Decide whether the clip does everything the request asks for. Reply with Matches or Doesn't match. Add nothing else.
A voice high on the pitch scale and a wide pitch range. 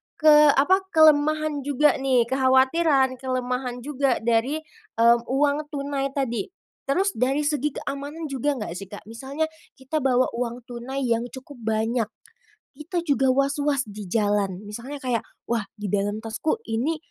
Doesn't match